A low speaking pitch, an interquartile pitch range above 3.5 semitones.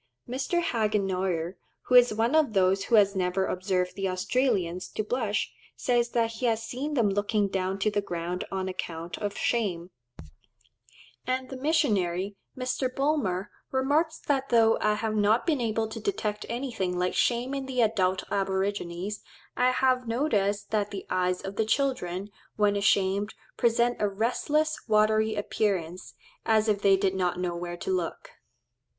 No: high, 210 Hz; average, 4.3 semitones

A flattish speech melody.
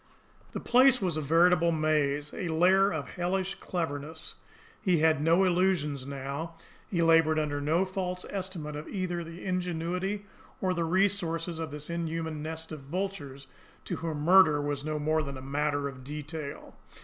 No: average, 3.3 semitones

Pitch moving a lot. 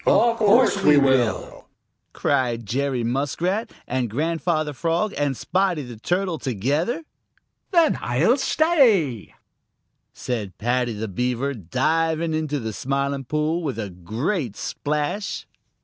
Yes: wide, 6.0 semitones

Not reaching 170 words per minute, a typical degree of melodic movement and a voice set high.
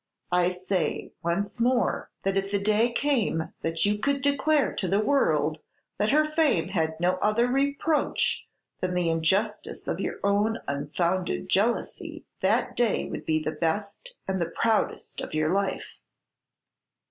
No: average, 150 wpm; wide, 5.7 semitones; high, 200 Hz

